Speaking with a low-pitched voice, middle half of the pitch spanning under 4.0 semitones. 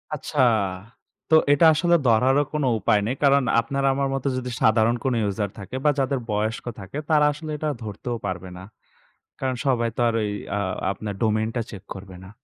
No: low, 120 Hz; average, 4.8 semitones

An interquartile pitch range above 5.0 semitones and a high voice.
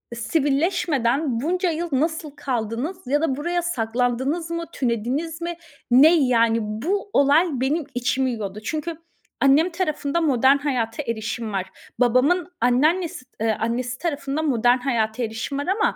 Yes: wide, 5.4 semitones; very high, 275 Hz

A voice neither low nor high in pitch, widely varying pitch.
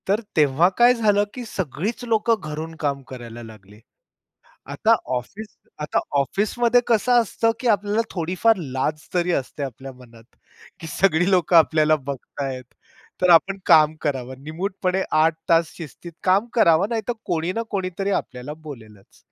Yes: medium, 165 Hz; wide, 6.4 semitones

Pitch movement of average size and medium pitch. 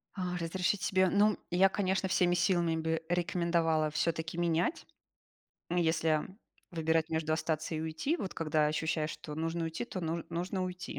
No: narrow, 2.2 semitones; medium, 170 Hz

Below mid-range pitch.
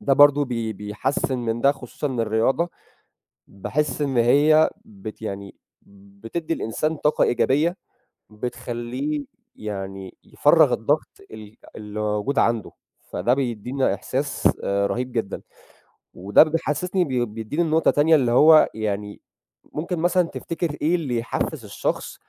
Yes: low, 125 Hz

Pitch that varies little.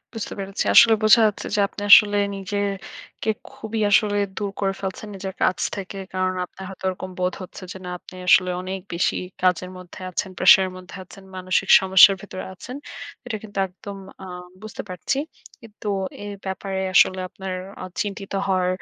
Yes: narrow, 1.8 semitones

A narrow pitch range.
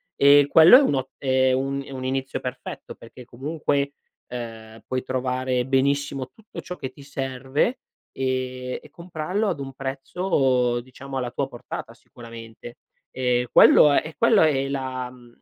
Yes: narrow, 1.9 semitones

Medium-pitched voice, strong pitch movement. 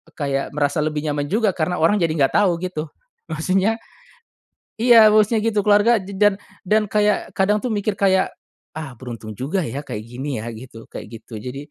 Yes: medium, 180 Hz; wide, 6.8 semitones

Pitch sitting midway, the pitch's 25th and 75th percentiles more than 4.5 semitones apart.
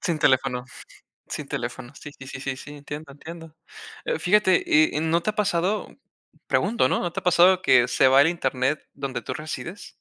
Yes: medium, 155 Hz; average, 4.9 semitones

